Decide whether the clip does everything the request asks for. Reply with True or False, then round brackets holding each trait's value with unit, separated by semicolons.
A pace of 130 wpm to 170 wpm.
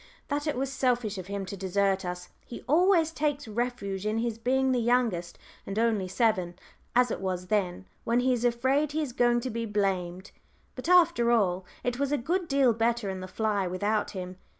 False (200 wpm)